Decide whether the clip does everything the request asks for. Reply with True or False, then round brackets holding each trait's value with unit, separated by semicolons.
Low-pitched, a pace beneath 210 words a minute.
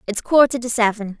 False (230 Hz; 200 wpm)